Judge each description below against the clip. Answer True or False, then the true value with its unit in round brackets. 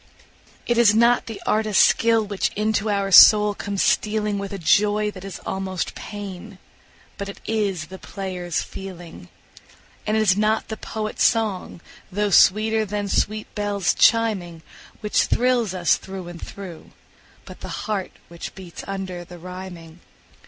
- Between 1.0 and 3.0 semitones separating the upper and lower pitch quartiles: True (2.5 semitones)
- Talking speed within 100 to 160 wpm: True (150 wpm)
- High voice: True (200 Hz)